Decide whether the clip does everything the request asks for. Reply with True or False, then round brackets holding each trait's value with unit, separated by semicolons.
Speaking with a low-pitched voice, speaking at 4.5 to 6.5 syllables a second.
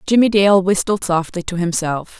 False (185 Hz; 4.8 syllables/s)